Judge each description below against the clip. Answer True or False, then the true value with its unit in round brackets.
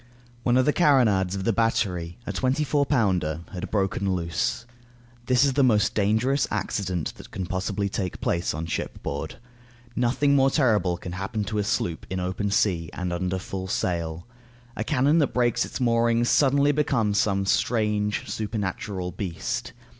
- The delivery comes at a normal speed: True (170 wpm)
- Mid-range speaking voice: False (105 Hz)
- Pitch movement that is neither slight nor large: True (5.0 semitones)